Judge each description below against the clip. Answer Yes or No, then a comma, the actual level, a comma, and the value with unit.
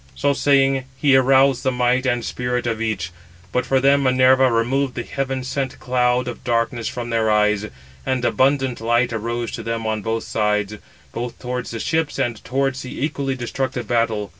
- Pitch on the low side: Yes, low, 125 Hz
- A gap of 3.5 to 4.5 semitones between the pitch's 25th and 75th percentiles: No, narrow, 2.4 semitones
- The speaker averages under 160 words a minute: No, average, 180 wpm